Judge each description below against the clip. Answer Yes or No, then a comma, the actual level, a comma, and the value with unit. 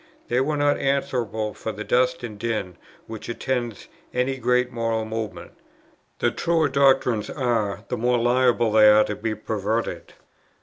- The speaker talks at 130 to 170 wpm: Yes, average, 155 wpm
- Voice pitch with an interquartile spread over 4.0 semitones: No, average, 2.8 semitones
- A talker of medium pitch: No, low, 120 Hz